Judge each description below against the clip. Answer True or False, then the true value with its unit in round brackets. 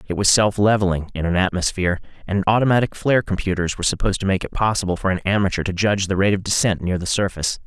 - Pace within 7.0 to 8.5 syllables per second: True (7.2 syllables/s)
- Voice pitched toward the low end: True (95 Hz)